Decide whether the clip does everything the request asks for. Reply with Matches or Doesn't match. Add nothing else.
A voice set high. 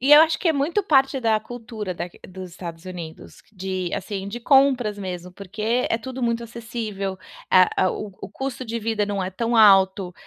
Matches